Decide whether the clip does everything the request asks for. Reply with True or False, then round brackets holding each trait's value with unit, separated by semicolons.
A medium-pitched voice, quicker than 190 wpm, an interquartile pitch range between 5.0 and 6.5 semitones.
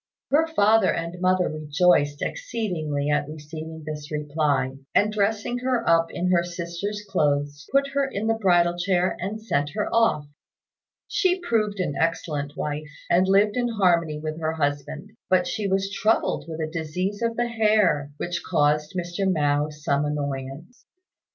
False (175 Hz; 155 wpm; 5.6 semitones)